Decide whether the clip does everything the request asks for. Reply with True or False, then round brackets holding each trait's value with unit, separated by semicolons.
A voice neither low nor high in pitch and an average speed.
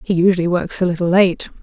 False (180 Hz; 220 wpm)